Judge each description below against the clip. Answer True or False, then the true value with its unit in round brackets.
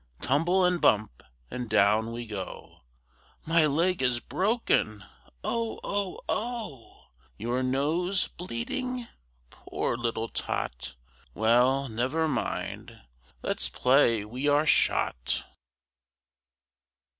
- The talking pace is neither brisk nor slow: False (100 wpm)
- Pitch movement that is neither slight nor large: False (7.5 semitones)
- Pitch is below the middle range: True (130 Hz)